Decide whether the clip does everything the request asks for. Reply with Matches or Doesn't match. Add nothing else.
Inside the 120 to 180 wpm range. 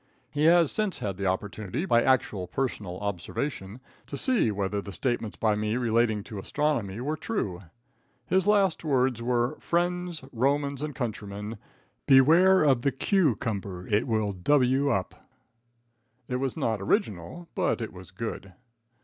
Matches